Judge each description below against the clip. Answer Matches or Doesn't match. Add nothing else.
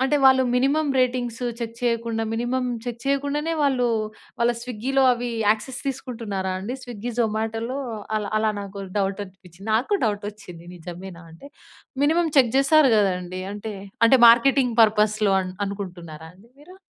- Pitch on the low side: Doesn't match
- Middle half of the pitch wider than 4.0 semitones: Matches